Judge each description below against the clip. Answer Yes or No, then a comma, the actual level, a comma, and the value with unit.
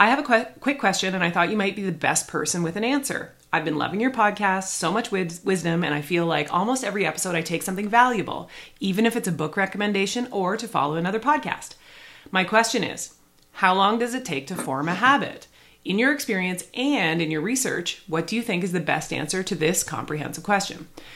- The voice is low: No, high, 190 Hz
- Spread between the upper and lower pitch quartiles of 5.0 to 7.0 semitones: Yes, average, 5.3 semitones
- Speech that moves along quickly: Yes, fast, 220 wpm